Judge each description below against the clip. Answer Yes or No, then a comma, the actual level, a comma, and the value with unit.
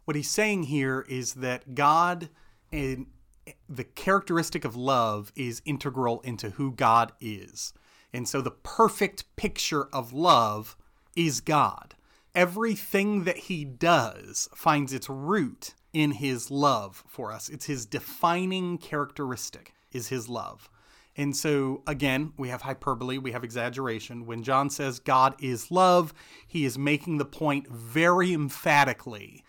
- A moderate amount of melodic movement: Yes, average, 4.6 semitones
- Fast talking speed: No, average, 140 wpm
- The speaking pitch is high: No, medium, 140 Hz